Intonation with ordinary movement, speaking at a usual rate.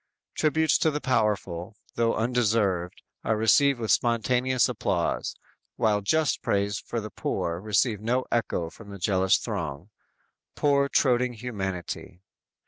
No: average, 4.1 semitones; slow, 130 wpm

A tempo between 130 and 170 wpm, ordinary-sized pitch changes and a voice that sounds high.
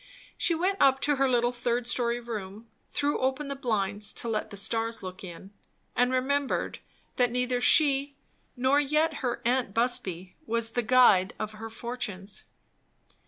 Yes: average, 160 wpm; average, 3.7 semitones; high, 245 Hz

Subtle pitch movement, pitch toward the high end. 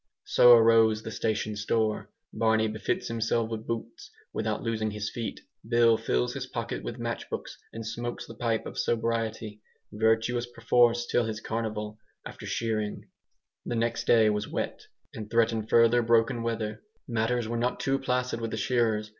No: narrow, 1.2 semitones; low, 115 Hz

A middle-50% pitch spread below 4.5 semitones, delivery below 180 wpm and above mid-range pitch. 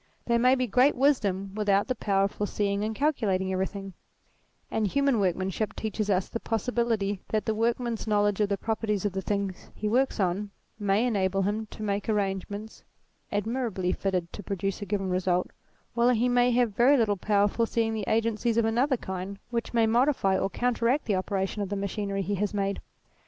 No: average, 2.9 semitones; average, 190 wpm; high, 210 Hz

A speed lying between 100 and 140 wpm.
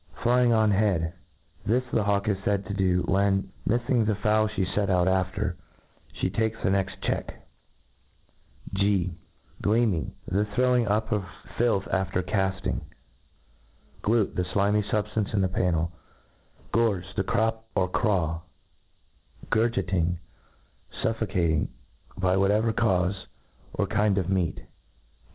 Yes: slow, 135 wpm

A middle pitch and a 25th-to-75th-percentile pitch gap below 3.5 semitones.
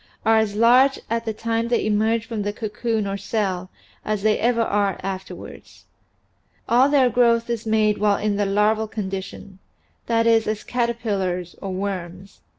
No: high, 215 Hz; narrow, 2.5 semitones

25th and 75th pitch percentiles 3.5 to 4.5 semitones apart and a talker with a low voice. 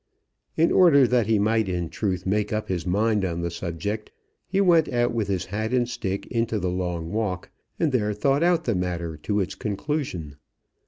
No: average, 4.9 semitones; low, 105 Hz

